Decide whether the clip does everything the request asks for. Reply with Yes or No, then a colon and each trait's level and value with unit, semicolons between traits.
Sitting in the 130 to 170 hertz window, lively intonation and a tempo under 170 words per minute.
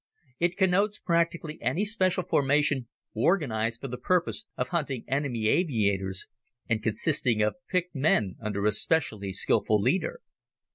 Yes: medium, 140 Hz; wide, 8.1 semitones; slow, 135 wpm